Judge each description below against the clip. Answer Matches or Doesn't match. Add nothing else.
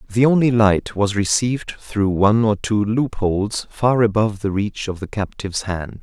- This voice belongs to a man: Matches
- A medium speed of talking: Matches